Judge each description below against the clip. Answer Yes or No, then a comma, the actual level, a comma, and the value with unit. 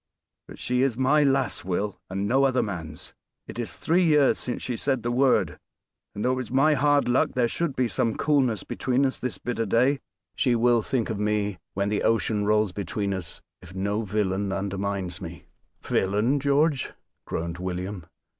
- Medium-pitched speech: No, low, 115 Hz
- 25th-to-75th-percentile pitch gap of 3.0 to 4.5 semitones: No, average, 4.9 semitones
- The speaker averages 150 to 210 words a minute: Yes, average, 185 wpm